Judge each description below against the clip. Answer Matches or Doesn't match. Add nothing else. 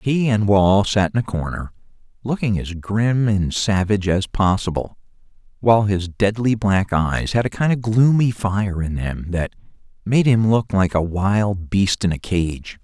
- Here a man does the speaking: Matches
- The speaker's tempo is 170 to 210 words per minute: Matches